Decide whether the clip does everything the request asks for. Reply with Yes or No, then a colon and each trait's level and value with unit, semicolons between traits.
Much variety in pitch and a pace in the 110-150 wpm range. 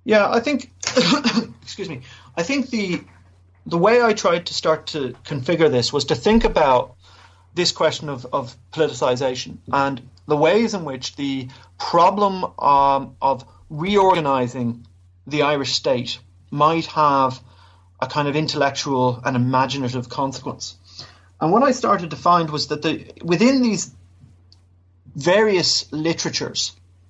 Yes: wide, 6.3 semitones; slow, 135 wpm